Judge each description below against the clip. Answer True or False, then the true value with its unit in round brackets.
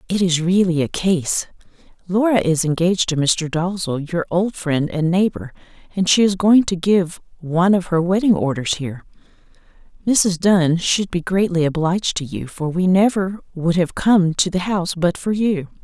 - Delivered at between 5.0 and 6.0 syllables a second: False (4.8 syllables/s)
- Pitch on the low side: False (175 Hz)